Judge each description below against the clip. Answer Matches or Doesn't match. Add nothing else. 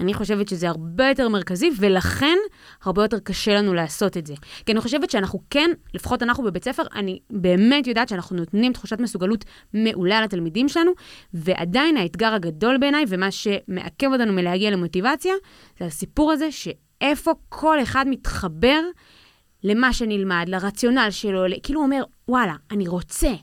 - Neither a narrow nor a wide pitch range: Doesn't match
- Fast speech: Matches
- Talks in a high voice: Matches